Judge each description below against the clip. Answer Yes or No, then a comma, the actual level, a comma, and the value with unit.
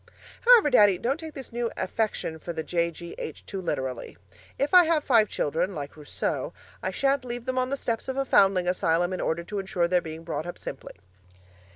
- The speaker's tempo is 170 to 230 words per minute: Yes, average, 200 wpm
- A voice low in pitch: No, high, 195 Hz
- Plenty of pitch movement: Yes, wide, 7.2 semitones